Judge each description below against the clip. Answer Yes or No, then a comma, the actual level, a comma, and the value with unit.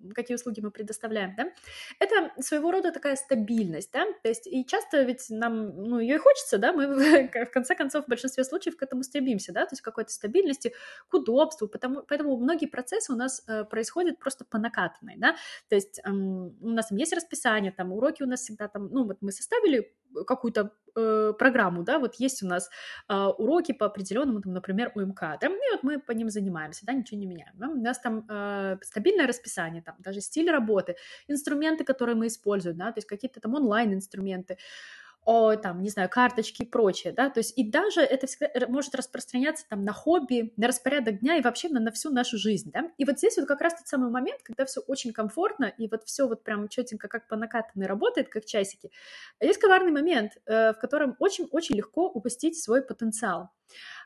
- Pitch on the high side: Yes, high, 245 Hz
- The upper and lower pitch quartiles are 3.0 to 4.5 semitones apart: No, average, 4.9 semitones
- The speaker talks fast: Yes, fast, 200 wpm